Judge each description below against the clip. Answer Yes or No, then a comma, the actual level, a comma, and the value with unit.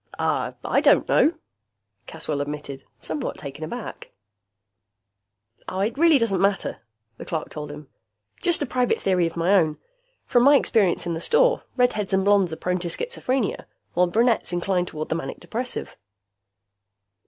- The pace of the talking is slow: No, average, 150 wpm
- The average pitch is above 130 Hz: Yes, high, 190 Hz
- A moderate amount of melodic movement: No, wide, 6.9 semitones